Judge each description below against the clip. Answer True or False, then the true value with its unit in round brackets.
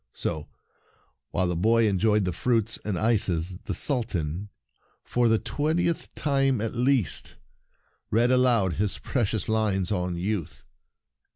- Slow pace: True (125 wpm)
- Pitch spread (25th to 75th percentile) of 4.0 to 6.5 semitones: True (4.7 semitones)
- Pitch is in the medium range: False (110 Hz)